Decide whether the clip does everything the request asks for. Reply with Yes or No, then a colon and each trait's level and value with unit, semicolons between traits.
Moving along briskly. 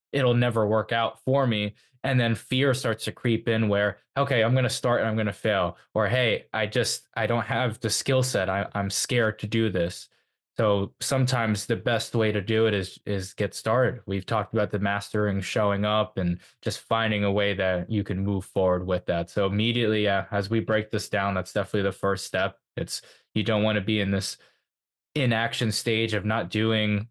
Yes: fast, 215 wpm